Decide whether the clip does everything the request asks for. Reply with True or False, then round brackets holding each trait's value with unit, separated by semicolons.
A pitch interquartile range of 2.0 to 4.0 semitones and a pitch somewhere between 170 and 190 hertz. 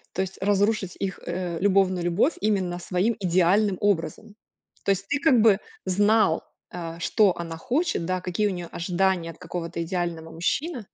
True (3.1 semitones; 185 Hz)